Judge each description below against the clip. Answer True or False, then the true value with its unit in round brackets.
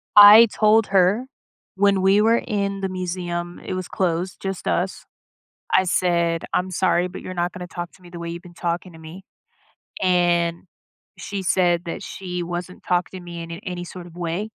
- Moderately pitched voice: True (180 Hz)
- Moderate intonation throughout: False (1.8 semitones)